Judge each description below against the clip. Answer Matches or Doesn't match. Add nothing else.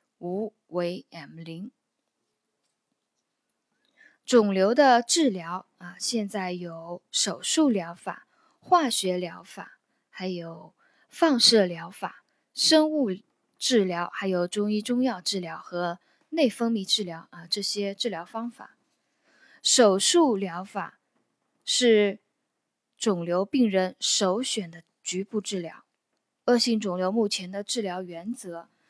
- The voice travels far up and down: Doesn't match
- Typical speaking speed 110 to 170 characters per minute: Matches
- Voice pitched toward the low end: Doesn't match